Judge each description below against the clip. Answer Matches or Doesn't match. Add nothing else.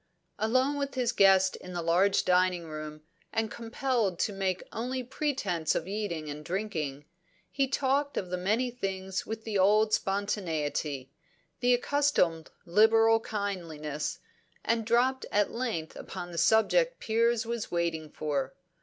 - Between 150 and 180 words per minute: Doesn't match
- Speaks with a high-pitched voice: Matches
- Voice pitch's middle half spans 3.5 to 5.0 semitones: Doesn't match